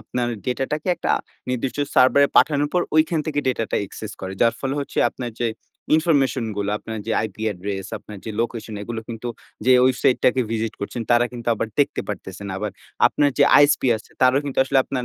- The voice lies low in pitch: Yes, low, 120 Hz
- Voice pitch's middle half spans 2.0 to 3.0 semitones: No, average, 3.9 semitones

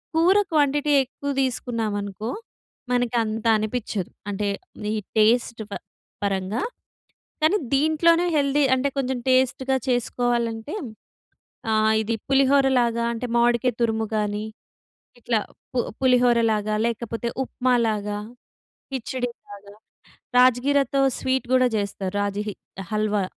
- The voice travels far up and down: No, average, 3.5 semitones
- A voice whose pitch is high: Yes, high, 240 Hz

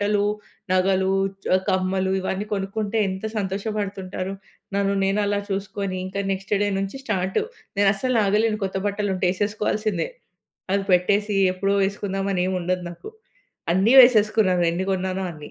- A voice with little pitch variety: Yes, narrow, 1.5 semitones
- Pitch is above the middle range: Yes, high, 195 Hz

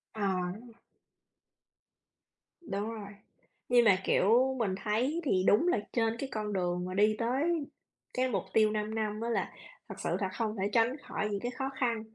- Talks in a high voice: Yes, high, 220 Hz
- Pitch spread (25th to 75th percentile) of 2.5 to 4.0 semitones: Yes, average, 3.5 semitones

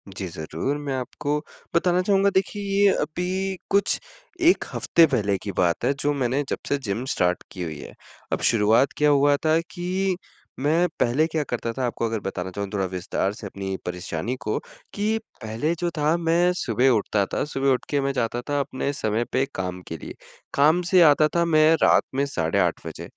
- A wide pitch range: Yes, wide, 8.1 semitones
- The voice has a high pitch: No, medium, 140 Hz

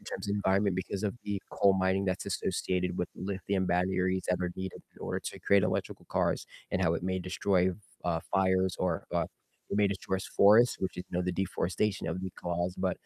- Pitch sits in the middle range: No, very low, 95 Hz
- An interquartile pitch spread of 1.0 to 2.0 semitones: Yes, narrow, 1.3 semitones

